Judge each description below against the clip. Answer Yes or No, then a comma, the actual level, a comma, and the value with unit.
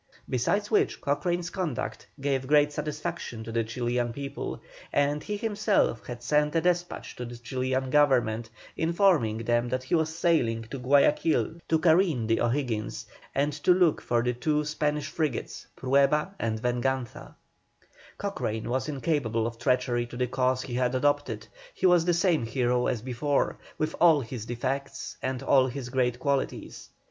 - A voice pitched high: No, low, 135 Hz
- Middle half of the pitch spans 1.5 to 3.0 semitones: No, average, 4.1 semitones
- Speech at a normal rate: Yes, average, 160 wpm